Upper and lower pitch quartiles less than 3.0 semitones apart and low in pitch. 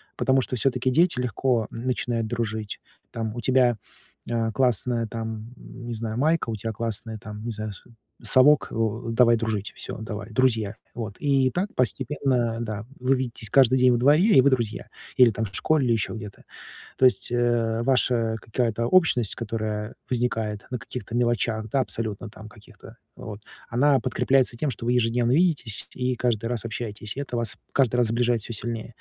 Yes: narrow, 2.4 semitones; low, 115 Hz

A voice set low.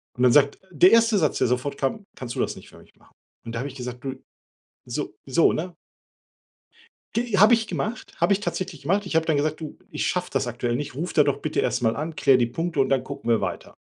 No: medium, 145 Hz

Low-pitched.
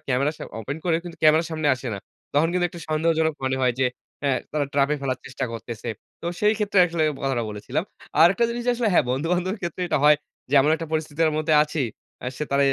No: medium, 155 Hz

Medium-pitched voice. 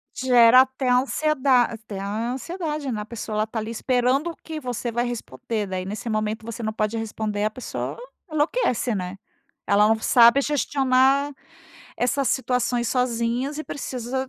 No: high, 245 Hz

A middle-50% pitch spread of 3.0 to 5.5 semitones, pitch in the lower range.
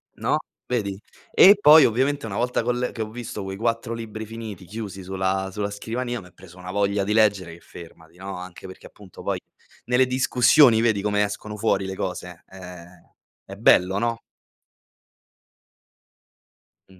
Yes: average, 3.6 semitones; low, 105 Hz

